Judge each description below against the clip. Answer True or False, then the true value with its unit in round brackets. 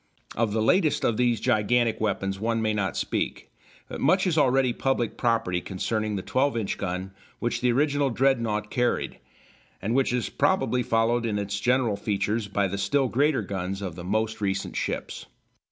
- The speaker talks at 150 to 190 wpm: True (175 wpm)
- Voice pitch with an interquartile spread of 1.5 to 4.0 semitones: True (3.7 semitones)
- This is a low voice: True (115 Hz)